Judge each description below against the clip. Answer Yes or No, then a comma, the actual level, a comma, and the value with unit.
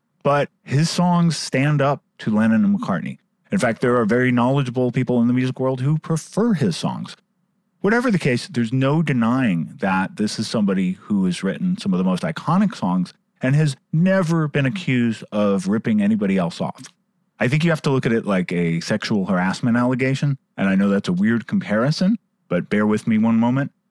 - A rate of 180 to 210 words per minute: Yes, average, 200 wpm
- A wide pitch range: Yes, wide, 7.6 semitones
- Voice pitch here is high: No, medium, 155 Hz